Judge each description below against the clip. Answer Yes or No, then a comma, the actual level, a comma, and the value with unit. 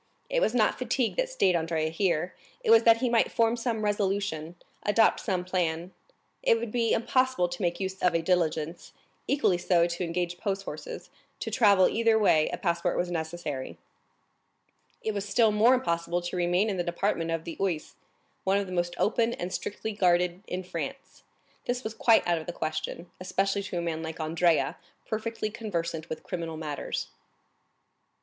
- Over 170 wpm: Yes, average, 180 wpm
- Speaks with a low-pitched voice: No, medium, 185 Hz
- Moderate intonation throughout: Yes, average, 4.4 semitones